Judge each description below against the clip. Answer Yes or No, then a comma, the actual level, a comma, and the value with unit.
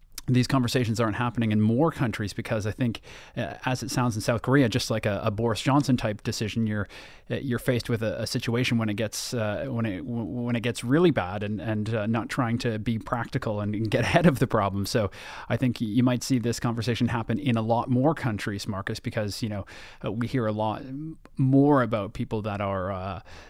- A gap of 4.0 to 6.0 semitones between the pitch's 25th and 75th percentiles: No, narrow, 2.6 semitones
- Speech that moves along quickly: Yes, fast, 220 wpm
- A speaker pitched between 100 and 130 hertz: Yes, low, 115 Hz